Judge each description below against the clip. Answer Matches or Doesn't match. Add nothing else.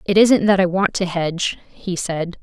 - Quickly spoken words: Matches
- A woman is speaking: Matches